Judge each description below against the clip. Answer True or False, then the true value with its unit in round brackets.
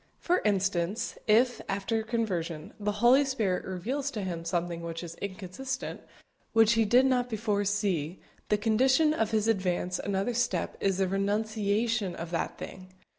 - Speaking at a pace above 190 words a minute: False (155 wpm)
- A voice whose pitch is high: True (205 Hz)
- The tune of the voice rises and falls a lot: False (3.8 semitones)